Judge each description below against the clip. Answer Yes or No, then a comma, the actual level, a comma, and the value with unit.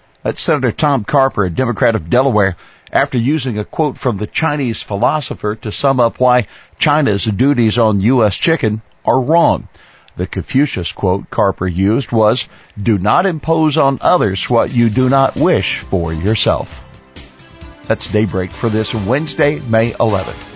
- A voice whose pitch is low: Yes, low, 115 Hz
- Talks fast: No, average, 150 wpm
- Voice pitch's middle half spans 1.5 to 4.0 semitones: No, average, 4.6 semitones